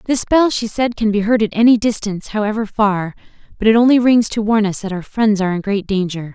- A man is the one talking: No, female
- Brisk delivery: Yes, fast, 245 wpm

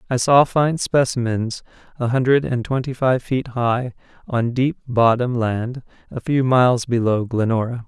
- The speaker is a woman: No, male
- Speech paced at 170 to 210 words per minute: No, average, 150 wpm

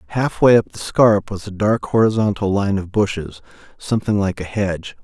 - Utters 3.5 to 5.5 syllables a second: Yes, 5.2 syllables/s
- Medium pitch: No, low, 100 Hz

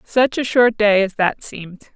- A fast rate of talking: Yes, fast, 215 wpm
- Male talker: No, female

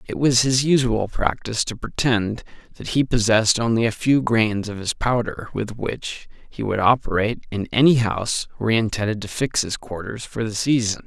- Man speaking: Yes, male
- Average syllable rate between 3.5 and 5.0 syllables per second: No, 5.2 syllables/s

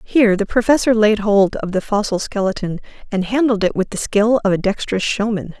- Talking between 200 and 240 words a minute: Yes, fast, 205 wpm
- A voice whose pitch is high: Yes, high, 210 Hz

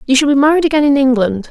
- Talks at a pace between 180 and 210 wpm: No, fast, 280 wpm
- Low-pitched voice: No, very high, 270 Hz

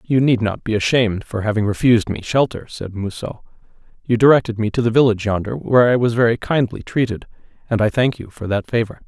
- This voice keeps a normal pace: No, fast, 210 wpm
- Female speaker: No, male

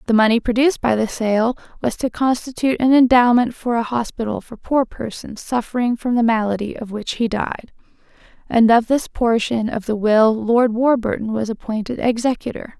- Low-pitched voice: No, high, 235 Hz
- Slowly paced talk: No, average, 175 wpm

